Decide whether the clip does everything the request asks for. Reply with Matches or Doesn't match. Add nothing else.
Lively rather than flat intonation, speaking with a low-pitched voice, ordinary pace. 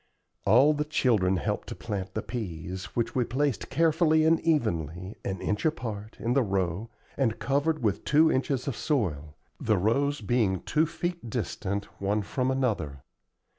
Matches